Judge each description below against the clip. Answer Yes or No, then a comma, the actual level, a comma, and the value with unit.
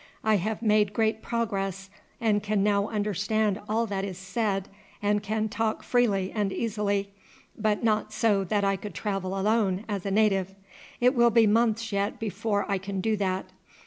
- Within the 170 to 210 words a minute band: Yes, average, 175 wpm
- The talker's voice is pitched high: Yes, high, 205 Hz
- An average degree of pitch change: No, narrow, 1.9 semitones